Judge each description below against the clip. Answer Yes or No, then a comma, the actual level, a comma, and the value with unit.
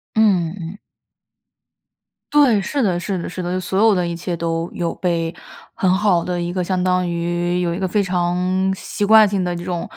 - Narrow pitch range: Yes, narrow, 1.9 semitones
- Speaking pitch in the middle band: Yes, medium, 180 Hz